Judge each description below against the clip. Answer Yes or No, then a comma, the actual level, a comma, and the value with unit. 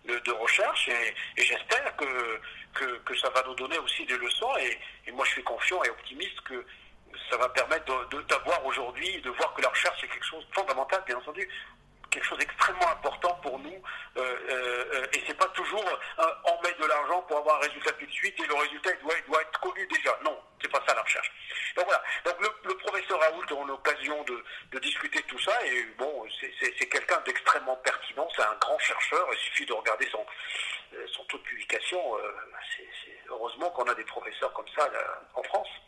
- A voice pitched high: No, medium, 155 Hz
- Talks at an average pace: No, fast, 225 wpm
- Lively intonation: Yes, wide, 7.5 semitones